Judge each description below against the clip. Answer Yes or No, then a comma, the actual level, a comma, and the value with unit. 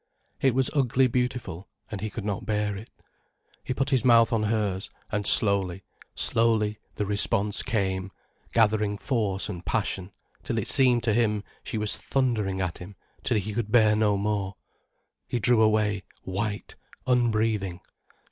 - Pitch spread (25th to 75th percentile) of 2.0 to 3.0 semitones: Yes, narrow, 2.6 semitones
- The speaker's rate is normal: Yes, average, 155 wpm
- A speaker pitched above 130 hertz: No, low, 105 Hz